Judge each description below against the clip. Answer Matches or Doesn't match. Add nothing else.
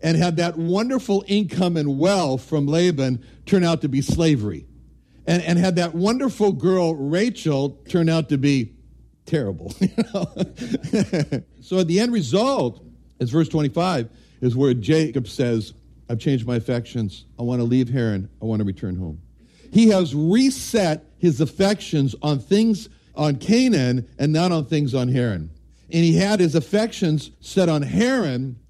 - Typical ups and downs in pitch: Doesn't match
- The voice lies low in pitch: Doesn't match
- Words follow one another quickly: Doesn't match